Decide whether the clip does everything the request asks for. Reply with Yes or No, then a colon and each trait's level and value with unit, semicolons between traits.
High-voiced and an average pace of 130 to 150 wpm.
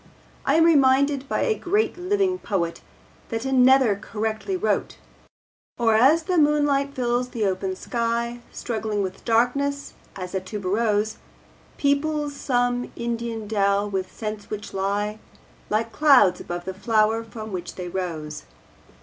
Yes: high, 230 Hz; slow, 135 wpm